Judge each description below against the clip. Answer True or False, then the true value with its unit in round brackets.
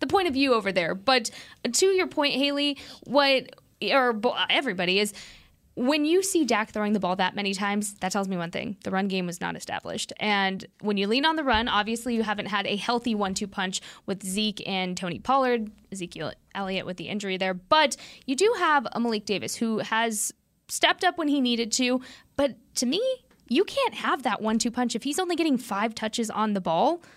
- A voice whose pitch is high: True (230 Hz)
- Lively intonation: True (5.7 semitones)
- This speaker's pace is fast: True (210 wpm)